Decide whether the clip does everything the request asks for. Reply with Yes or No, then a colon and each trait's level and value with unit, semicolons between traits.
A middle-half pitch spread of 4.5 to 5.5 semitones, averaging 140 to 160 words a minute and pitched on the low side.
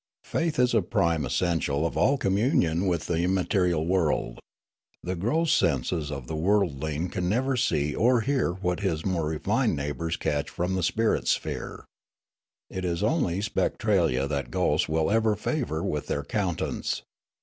Yes: average, 5.0 semitones; average, 155 wpm; very low, 90 Hz